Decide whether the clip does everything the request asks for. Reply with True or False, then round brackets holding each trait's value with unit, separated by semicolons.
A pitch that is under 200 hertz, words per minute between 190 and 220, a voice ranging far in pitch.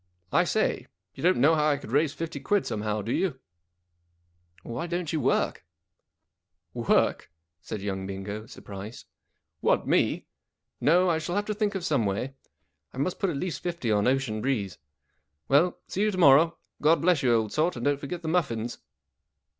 True (140 Hz; 195 wpm; 8.0 semitones)